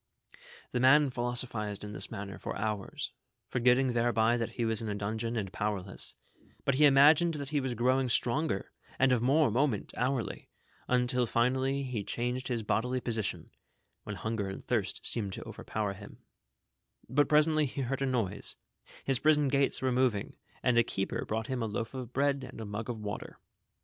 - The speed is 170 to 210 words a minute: Yes, average, 180 wpm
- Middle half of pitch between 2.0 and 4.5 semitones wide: Yes, average, 3.3 semitones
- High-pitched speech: No, low, 120 Hz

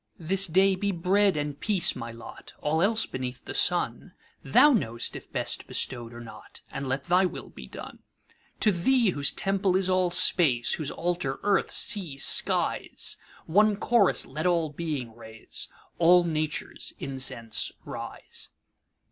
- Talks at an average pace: No, slow, 130 wpm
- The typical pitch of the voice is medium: Yes, medium, 170 Hz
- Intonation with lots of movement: Yes, wide, 6.2 semitones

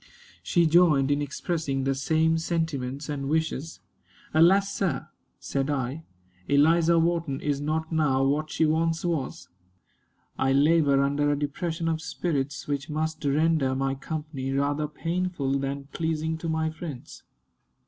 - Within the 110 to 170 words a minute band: Yes, average, 140 wpm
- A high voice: No, medium, 155 Hz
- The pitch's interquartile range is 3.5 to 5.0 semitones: No, average, 2.7 semitones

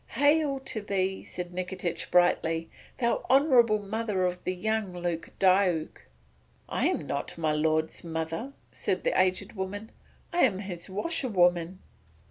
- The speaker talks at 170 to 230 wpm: No, slow, 135 wpm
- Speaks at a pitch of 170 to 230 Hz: Yes, high, 190 Hz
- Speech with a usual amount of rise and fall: Yes, average, 4.0 semitones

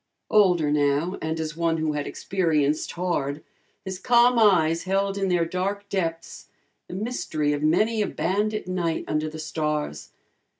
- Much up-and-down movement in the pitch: No, average, 4.2 semitones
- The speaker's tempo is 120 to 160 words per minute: Yes, average, 155 wpm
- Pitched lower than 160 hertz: No, medium, 170 Hz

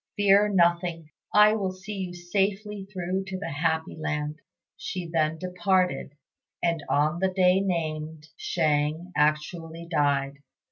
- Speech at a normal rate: No, slow, 130 wpm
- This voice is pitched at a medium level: Yes, medium, 175 Hz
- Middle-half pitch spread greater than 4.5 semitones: No, average, 3.5 semitones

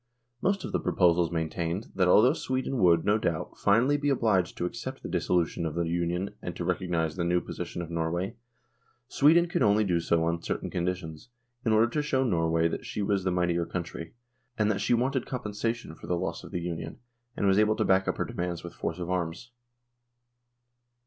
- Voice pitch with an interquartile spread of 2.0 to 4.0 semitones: No, average, 4.8 semitones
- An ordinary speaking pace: No, fast, 210 wpm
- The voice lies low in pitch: Yes, very low, 90 Hz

